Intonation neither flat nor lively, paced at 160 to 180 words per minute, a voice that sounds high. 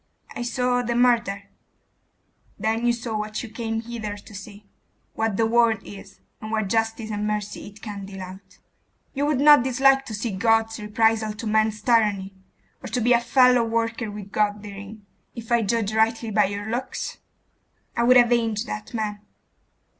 No: narrow, 2.2 semitones; average, 175 wpm; high, 220 Hz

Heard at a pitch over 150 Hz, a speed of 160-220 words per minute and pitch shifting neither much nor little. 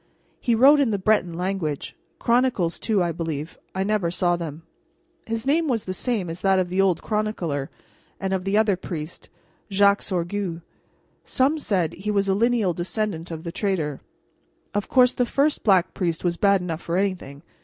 Yes: high, 190 Hz; average, 180 wpm; average, 3.9 semitones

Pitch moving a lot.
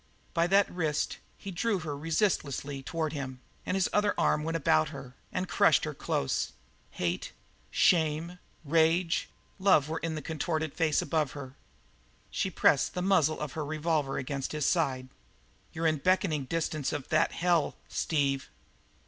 No: average, 3.1 semitones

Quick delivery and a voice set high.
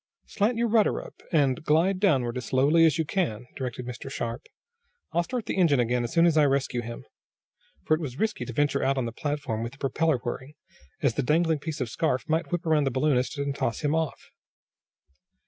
No: fast, 215 wpm; medium, 145 Hz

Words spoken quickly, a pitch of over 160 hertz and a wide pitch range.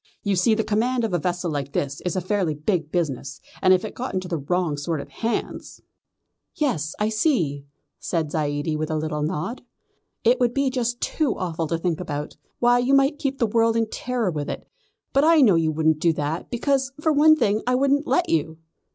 Yes: fast, 215 wpm; medium, 185 Hz; wide, 7.7 semitones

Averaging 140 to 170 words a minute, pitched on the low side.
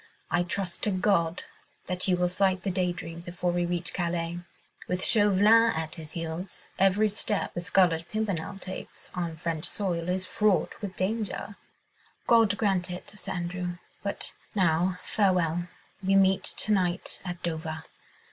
No: average, 155 wpm; medium, 180 Hz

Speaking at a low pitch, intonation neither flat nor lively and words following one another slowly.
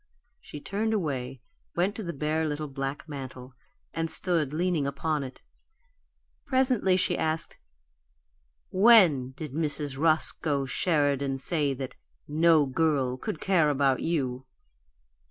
No: medium, 150 Hz; average, 3.8 semitones; slow, 120 wpm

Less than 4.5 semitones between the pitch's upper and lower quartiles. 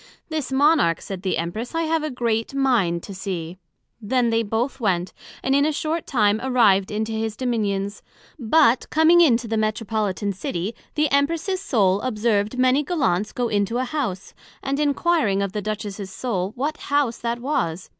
No: wide, 5.5 semitones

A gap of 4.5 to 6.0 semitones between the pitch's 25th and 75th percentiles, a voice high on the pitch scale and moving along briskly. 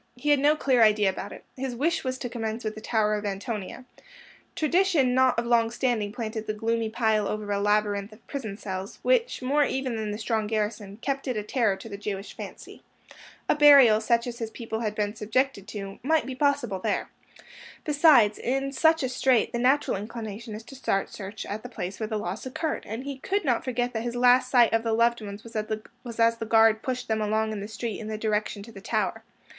No: average, 3.3 semitones; high, 225 Hz; fast, 220 wpm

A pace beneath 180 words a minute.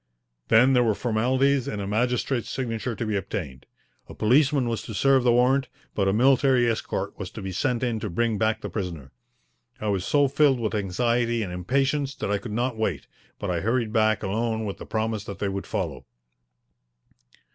No: average, 195 wpm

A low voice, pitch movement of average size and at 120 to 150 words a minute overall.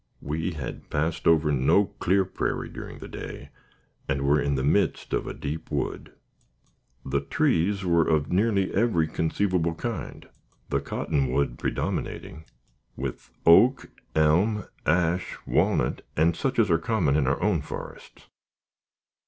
Yes: very low, 80 Hz; average, 4.6 semitones; slow, 135 wpm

